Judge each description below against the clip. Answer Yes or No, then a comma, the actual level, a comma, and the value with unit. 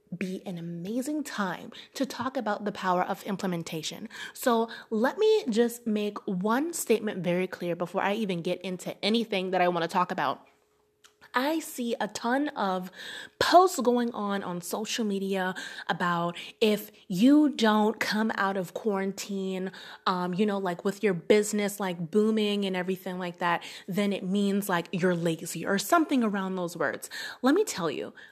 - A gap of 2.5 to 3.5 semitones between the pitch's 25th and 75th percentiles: No, average, 4.1 semitones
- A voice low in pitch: No, high, 200 Hz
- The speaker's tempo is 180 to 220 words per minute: No, average, 165 wpm